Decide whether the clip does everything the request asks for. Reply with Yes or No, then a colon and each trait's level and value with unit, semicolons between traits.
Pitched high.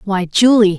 Yes: high, 205 Hz